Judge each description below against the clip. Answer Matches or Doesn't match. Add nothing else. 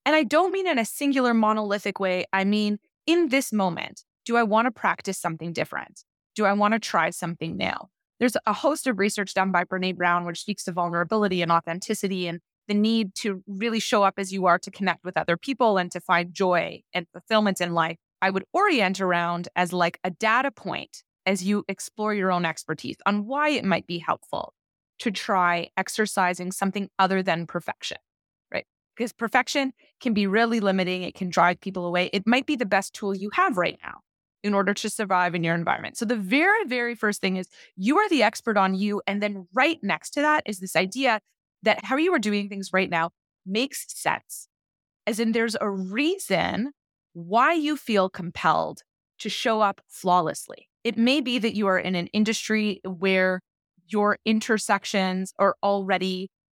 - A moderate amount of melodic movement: Matches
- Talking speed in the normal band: Matches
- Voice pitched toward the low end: Doesn't match